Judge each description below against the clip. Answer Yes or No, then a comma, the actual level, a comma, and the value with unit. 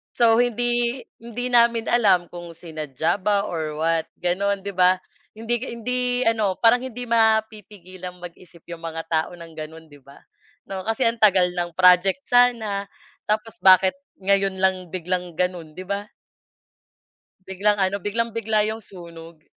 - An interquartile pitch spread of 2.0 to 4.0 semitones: No, average, 4.4 semitones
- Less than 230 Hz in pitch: Yes, high, 190 Hz